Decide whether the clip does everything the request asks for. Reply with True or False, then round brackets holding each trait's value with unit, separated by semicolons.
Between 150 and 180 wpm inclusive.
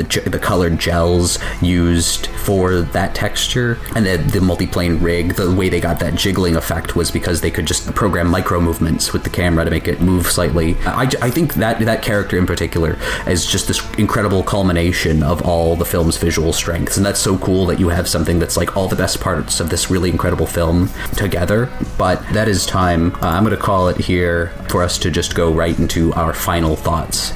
False (205 wpm)